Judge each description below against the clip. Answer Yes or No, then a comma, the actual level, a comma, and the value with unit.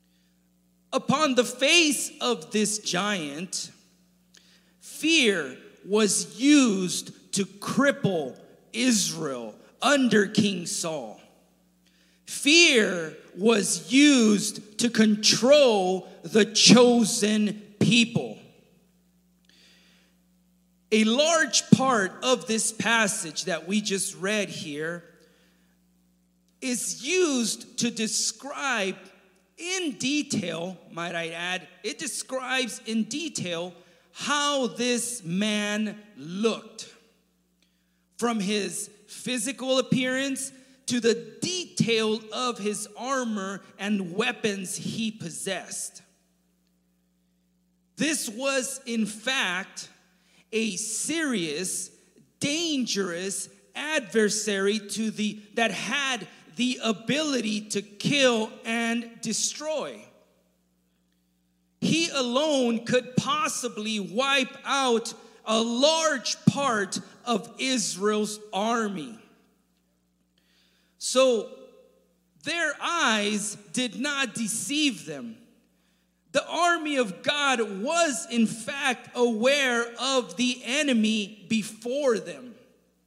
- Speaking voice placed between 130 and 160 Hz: No, high, 220 Hz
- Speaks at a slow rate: Yes, slow, 85 wpm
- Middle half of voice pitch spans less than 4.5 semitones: No, average, 5.2 semitones